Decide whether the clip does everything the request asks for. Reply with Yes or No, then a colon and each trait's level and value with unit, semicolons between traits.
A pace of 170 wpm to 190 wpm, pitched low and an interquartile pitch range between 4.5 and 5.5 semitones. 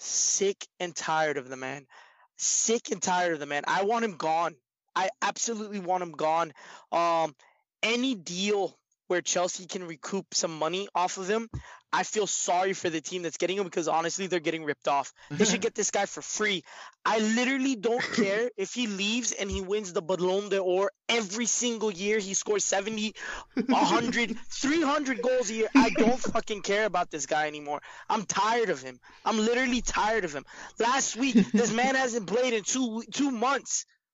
No: average, 185 wpm; high, 205 Hz; average, 4.8 semitones